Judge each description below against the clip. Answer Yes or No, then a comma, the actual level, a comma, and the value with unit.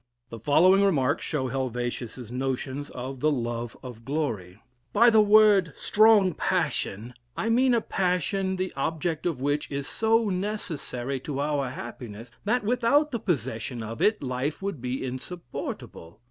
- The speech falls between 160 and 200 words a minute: No, average, 145 wpm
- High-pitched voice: No, medium, 145 Hz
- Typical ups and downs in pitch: No, wide, 7.8 semitones